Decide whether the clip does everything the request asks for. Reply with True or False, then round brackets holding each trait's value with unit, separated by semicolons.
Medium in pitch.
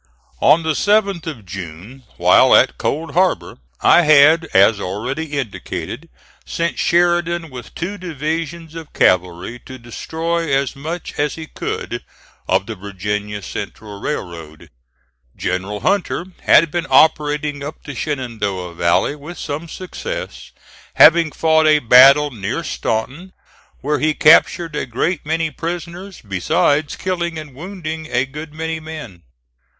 True (150 Hz)